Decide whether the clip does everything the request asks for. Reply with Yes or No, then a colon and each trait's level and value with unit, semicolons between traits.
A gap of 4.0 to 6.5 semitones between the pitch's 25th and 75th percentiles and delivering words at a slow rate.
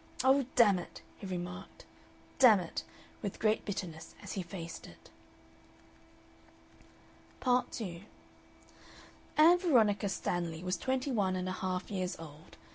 Yes: average, 5.1 semitones; slow, 120 wpm